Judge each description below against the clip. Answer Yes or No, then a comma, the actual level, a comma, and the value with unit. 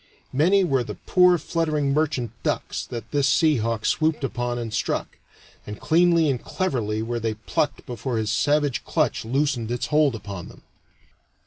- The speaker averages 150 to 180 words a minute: Yes, average, 160 wpm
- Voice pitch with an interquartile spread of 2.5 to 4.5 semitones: No, average, 4.9 semitones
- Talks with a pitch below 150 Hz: Yes, low, 135 Hz